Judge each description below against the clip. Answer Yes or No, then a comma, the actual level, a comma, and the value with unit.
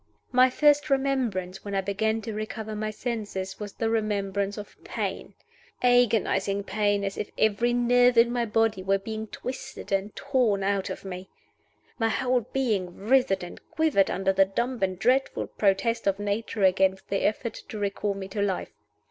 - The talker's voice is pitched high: Yes, high, 210 Hz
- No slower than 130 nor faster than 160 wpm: No, average, 170 wpm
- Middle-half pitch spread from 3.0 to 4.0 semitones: Yes, average, 3.5 semitones